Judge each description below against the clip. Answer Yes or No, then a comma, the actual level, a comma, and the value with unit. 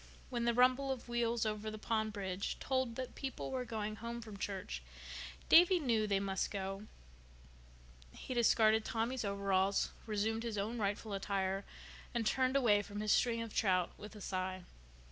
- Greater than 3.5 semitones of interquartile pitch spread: No, average, 3.0 semitones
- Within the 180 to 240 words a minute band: No, average, 165 wpm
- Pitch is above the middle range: Yes, high, 215 Hz